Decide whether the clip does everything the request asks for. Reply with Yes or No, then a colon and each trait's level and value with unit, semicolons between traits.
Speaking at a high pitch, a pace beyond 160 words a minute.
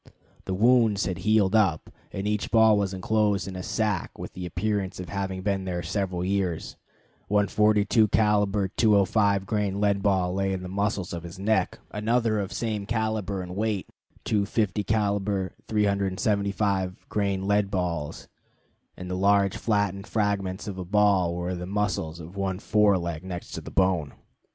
No: low, 100 Hz; average, 170 wpm